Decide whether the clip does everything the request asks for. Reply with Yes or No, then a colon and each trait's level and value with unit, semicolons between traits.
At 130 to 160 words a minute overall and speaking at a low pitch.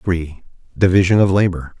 Yes: slow, 135 wpm; very low, 90 Hz